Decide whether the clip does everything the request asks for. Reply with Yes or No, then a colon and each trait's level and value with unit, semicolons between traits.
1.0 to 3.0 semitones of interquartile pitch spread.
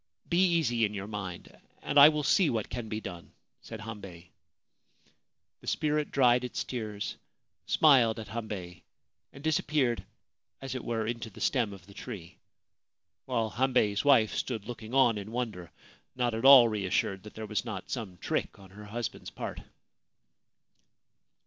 No: average, 3.8 semitones